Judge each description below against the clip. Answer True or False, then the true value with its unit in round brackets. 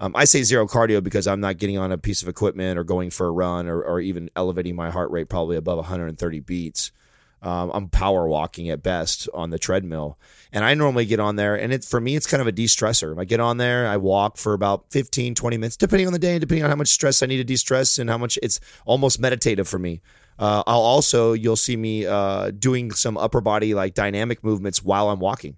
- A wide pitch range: False (4.8 semitones)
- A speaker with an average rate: False (245 wpm)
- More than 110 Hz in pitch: False (105 Hz)